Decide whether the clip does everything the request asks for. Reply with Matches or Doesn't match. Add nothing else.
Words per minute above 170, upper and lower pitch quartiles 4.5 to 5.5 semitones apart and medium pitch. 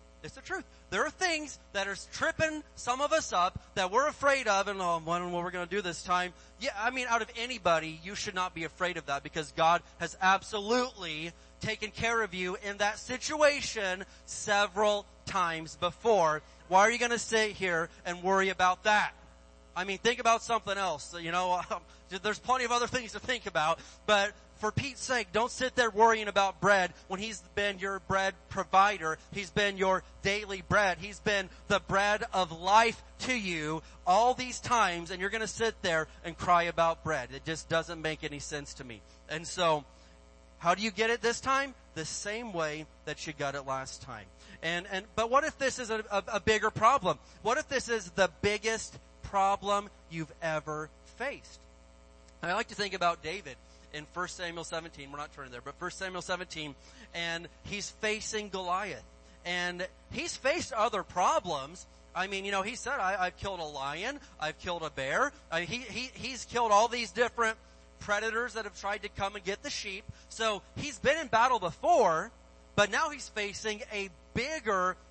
Doesn't match